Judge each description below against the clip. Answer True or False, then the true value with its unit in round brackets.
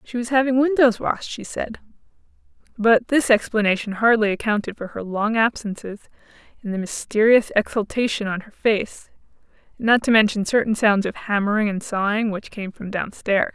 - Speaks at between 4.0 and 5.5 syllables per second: True (5.1 syllables/s)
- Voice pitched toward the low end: False (220 Hz)